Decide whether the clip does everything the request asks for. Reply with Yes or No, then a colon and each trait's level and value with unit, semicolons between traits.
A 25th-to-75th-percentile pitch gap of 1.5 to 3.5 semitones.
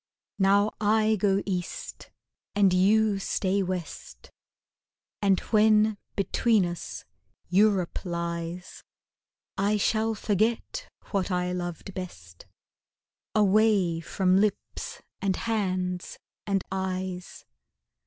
Yes: average, 2.8 semitones